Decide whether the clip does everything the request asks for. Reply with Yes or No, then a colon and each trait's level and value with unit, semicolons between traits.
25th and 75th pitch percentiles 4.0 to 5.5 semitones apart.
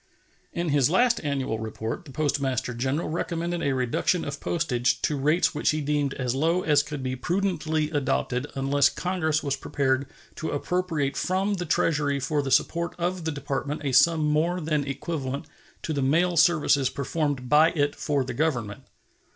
No: average, 3.4 semitones